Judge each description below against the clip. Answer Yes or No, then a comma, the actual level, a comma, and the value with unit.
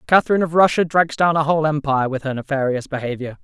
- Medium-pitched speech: Yes, medium, 150 Hz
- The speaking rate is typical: No, fast, 210 wpm